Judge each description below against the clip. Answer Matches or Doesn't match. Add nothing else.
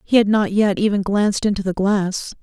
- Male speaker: Doesn't match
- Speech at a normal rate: Doesn't match